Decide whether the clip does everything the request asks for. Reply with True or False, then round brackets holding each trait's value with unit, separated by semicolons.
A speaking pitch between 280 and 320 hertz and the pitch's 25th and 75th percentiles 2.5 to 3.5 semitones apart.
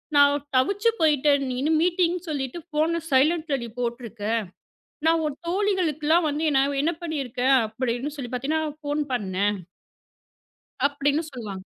False (290 Hz; 4.0 semitones)